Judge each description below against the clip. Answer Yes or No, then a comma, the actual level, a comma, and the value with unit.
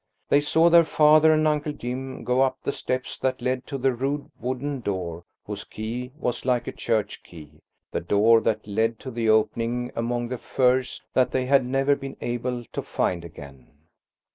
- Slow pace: No, average, 180 wpm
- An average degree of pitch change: Yes, average, 3.1 semitones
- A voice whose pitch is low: Yes, low, 125 Hz